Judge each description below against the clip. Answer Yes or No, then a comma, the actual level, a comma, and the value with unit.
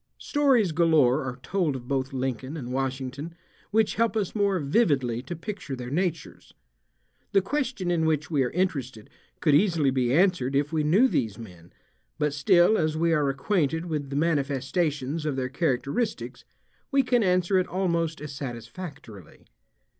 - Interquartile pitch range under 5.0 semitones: No, average, 5.3 semitones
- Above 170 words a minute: No, average, 160 wpm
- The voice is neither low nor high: Yes, medium, 150 Hz